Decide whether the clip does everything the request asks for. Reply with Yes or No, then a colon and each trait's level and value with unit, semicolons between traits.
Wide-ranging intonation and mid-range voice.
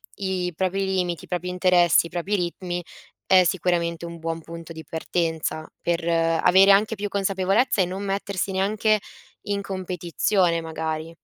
No: narrow, 2.5 semitones; medium, 180 Hz